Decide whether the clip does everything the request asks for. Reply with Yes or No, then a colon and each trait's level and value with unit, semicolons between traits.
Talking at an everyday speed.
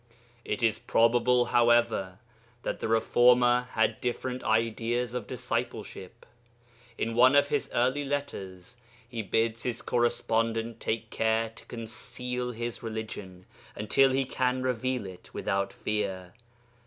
No: slow, 125 wpm